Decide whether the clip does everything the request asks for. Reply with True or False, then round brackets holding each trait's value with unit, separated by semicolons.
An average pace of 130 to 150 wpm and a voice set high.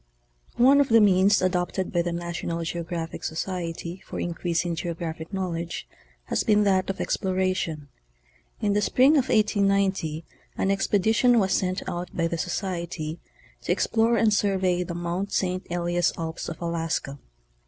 False (145 wpm; 180 Hz)